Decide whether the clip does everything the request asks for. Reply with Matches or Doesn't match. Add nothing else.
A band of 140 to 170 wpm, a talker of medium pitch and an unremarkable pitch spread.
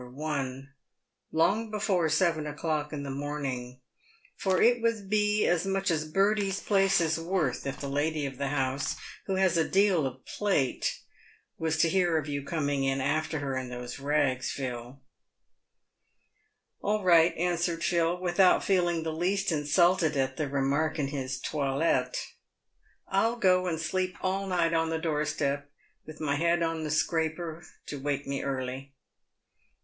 Matches